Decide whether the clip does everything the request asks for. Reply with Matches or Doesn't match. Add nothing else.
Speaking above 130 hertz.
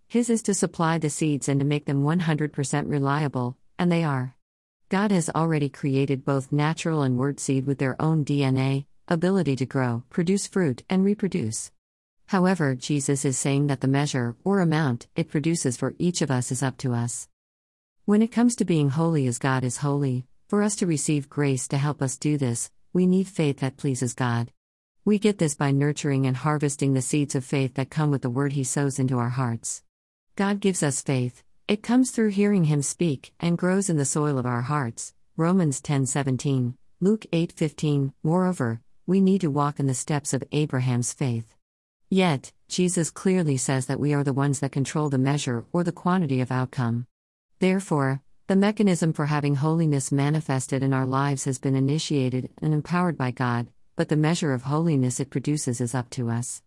Matches